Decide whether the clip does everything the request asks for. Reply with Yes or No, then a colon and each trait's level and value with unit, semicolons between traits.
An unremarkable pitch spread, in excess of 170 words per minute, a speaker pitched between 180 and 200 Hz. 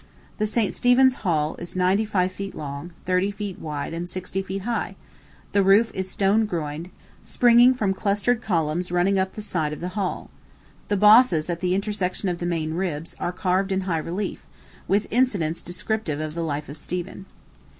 Yes: average, 3.3 semitones; average, 180 wpm; medium, 185 Hz